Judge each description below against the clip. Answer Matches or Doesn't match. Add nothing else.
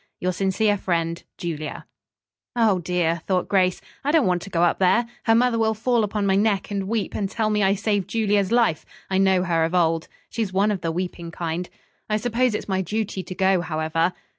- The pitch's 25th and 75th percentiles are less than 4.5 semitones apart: Matches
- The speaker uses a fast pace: Matches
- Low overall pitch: Doesn't match